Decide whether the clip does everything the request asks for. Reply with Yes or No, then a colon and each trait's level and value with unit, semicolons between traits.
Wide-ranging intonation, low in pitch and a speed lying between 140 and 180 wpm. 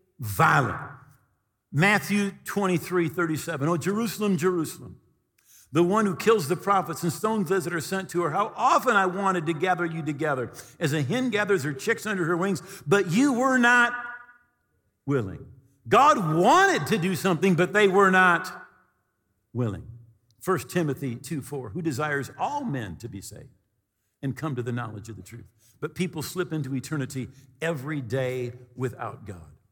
No: wide, 7.2 semitones; medium, 165 Hz; average, 165 wpm